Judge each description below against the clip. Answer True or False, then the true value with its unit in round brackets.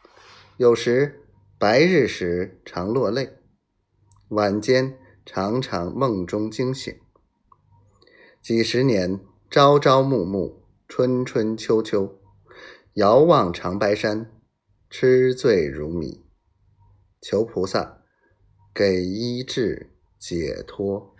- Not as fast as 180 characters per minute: True (125 characters per minute)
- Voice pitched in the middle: False (105 Hz)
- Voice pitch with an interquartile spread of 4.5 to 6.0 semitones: True (4.8 semitones)